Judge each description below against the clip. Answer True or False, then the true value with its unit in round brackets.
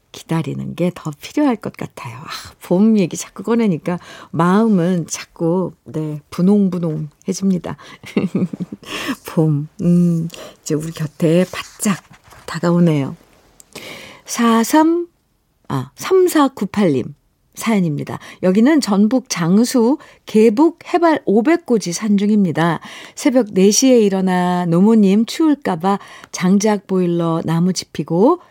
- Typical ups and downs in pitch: True (5.0 semitones)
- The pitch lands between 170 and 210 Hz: True (190 Hz)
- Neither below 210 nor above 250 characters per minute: True (215 characters per minute)